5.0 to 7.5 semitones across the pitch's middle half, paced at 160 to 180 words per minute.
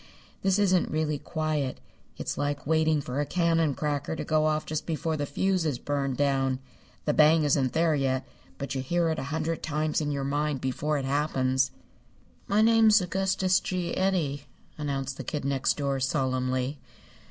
No: average, 2.9 semitones; average, 175 wpm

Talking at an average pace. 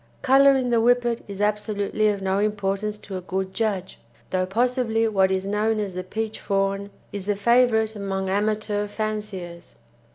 Yes: average, 165 wpm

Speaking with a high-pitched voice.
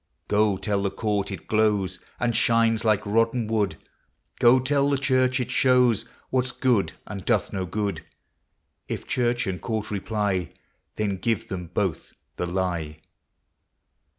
No: low, 105 Hz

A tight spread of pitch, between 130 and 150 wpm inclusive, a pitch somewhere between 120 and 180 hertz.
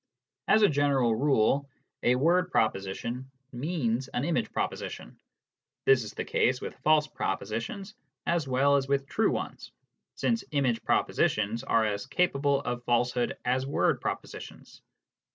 No: average, 3.3 semitones; average, 145 wpm; low, 135 Hz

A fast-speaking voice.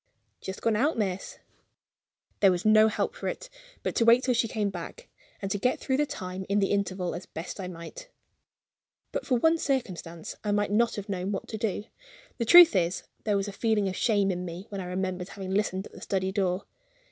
Yes: fast, 215 wpm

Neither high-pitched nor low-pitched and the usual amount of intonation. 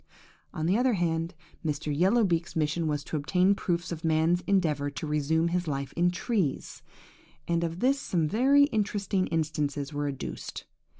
Yes: medium, 165 Hz; average, 3.8 semitones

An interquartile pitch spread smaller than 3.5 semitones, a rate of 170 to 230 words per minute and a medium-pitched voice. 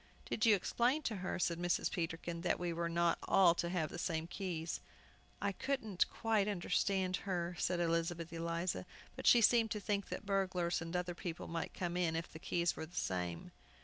Yes: average, 2.7 semitones; average, 195 wpm; medium, 175 Hz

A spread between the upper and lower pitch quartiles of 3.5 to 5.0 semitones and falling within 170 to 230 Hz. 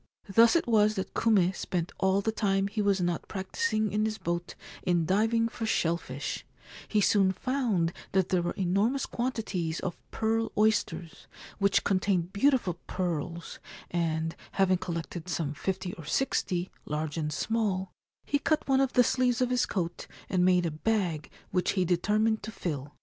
Yes: average, 4.1 semitones; high, 190 Hz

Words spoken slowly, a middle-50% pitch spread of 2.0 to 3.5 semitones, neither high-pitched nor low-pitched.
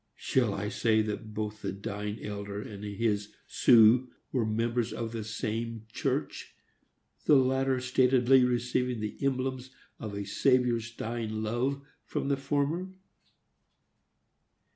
No: slow, 125 wpm; average, 3.2 semitones; low, 115 Hz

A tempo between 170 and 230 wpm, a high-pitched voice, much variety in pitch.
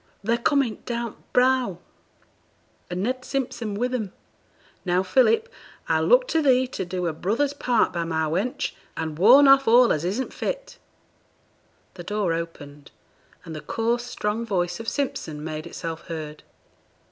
No: average, 155 wpm; high, 215 Hz; wide, 7.0 semitones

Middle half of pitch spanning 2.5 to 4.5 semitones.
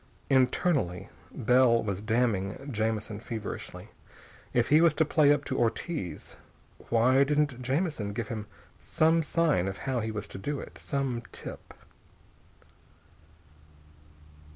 No: average, 5.0 semitones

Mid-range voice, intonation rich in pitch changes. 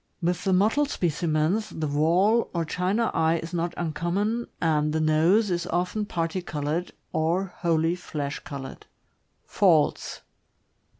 No: medium, 170 Hz; average, 3.1 semitones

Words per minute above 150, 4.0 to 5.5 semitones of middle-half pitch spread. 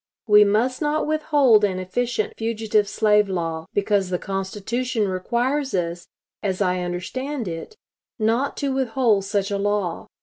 No: average, 140 wpm; average, 4.6 semitones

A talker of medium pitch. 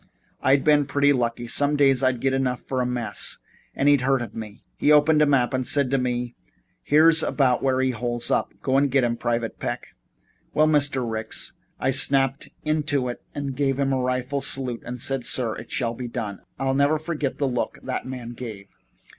No: low, 130 Hz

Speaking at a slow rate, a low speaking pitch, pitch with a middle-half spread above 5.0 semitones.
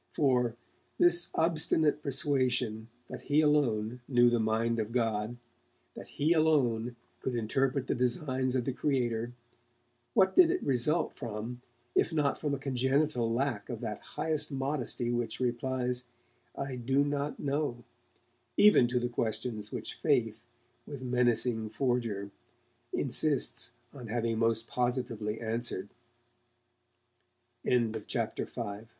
No: slow, 130 wpm; low, 125 Hz; average, 3.3 semitones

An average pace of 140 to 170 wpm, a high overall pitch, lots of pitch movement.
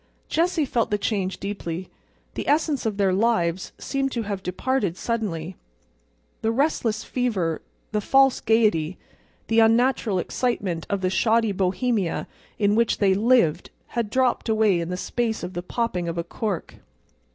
No: average, 155 wpm; high, 210 Hz; average, 4.3 semitones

